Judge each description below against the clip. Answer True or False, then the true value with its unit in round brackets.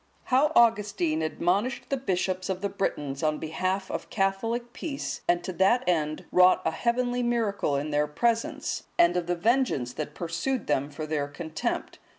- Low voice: False (185 Hz)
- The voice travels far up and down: True (7.1 semitones)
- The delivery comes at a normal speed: True (165 wpm)